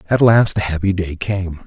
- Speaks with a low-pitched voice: Yes, very low, 95 Hz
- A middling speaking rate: No, fast, 215 wpm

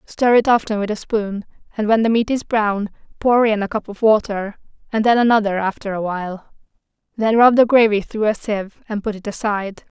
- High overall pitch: Yes, high, 215 Hz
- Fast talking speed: Yes, fast, 210 wpm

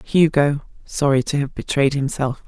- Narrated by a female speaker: Yes, female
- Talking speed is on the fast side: No, average, 145 wpm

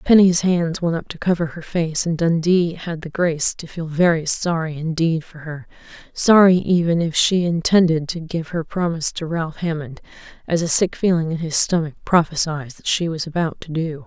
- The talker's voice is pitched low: No, medium, 165 Hz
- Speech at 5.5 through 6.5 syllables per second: No, 5.0 syllables/s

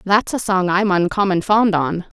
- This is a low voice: No, high, 190 Hz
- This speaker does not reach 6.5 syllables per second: Yes, 4.5 syllables/s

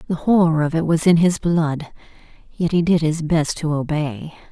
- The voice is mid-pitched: Yes, medium, 160 Hz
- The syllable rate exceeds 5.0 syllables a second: No, 4.7 syllables/s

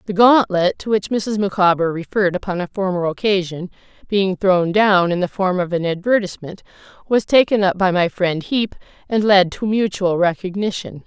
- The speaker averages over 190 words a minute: No, average, 180 wpm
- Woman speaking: Yes, female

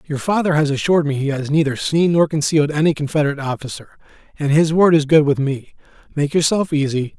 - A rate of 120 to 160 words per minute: No, average, 200 wpm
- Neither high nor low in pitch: Yes, medium, 150 Hz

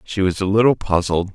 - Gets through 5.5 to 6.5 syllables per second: Yes, 5.7 syllables/s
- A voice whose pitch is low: Yes, very low, 95 Hz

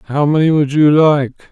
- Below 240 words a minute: Yes, average, 200 wpm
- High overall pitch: No, medium, 145 Hz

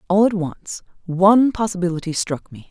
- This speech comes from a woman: Yes, female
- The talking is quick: No, average, 155 wpm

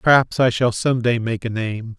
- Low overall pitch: Yes, low, 120 Hz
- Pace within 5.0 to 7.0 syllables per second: No, 4.8 syllables/s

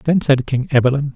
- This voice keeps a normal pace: No, fast, 210 wpm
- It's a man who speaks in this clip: Yes, male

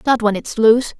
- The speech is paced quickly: Yes, fast, 240 wpm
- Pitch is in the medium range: No, high, 230 Hz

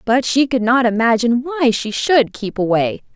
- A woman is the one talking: Yes, female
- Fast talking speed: No, average, 190 wpm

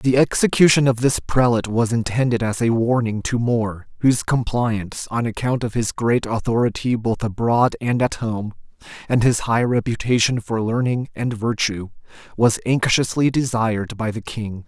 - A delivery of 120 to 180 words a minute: Yes, average, 160 wpm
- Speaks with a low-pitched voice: Yes, low, 115 Hz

